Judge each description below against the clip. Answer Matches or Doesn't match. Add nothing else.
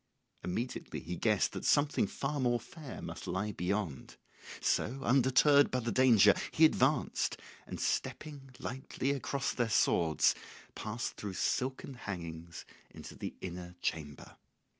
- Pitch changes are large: Matches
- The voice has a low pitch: Matches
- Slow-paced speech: Matches